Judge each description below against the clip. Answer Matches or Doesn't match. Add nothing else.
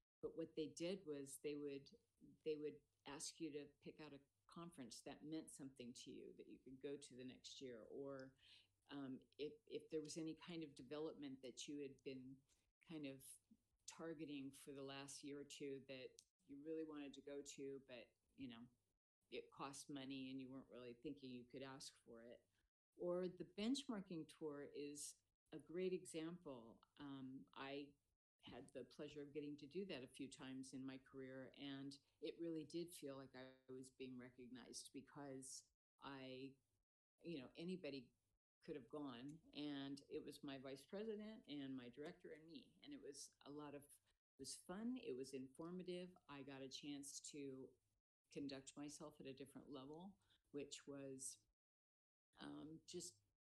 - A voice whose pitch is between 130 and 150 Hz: Matches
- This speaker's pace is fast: Doesn't match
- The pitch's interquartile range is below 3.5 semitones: Matches